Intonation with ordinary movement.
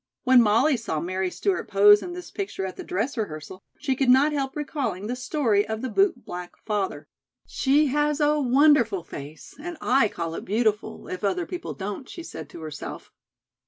No: wide, 7.4 semitones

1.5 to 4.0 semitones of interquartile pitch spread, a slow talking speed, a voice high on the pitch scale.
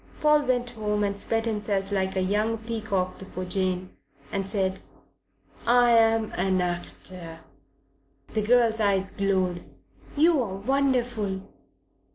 Yes: average, 3.3 semitones; slow, 125 wpm; high, 205 Hz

